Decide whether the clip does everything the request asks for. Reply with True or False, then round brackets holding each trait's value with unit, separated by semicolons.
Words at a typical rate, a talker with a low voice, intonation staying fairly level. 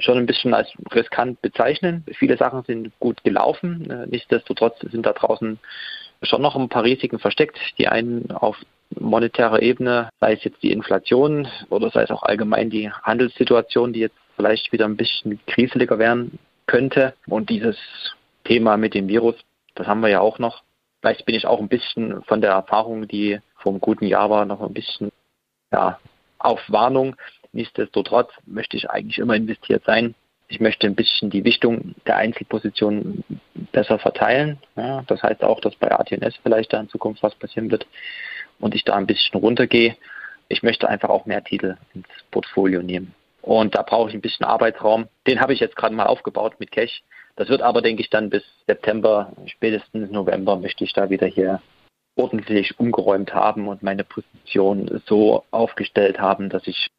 True (175 wpm; 115 Hz; 2.3 semitones)